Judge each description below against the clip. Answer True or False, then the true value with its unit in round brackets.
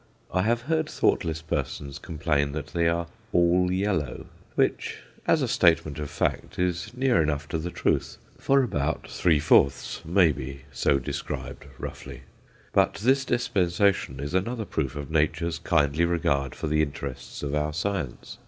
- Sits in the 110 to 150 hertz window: False (85 Hz)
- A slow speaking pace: False (155 wpm)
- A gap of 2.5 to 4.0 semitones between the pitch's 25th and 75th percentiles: False (4.4 semitones)